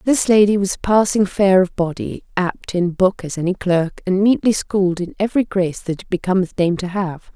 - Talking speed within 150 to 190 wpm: No, fast, 205 wpm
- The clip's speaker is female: Yes, female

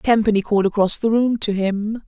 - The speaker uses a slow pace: No, average, 200 wpm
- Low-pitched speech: No, high, 215 Hz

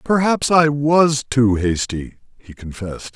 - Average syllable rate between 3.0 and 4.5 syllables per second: Yes, 4.1 syllables/s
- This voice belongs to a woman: No, male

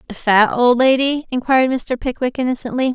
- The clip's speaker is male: No, female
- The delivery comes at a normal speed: Yes, average, 165 wpm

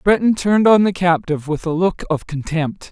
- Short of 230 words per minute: Yes, fast, 205 wpm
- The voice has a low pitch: No, medium, 175 Hz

